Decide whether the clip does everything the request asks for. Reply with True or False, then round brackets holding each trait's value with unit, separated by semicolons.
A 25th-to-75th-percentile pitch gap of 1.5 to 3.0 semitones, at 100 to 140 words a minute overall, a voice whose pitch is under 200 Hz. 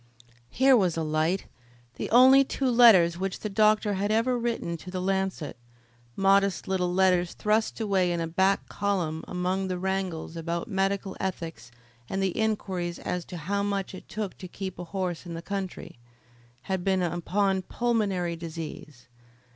False (2.6 semitones; 165 wpm; 190 Hz)